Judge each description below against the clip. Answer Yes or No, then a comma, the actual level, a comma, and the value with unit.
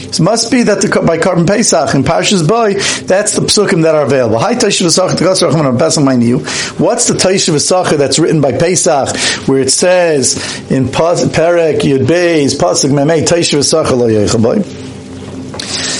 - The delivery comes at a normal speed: Yes, average, 180 wpm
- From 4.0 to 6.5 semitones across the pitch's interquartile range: Yes, average, 5.0 semitones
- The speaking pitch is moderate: Yes, medium, 170 Hz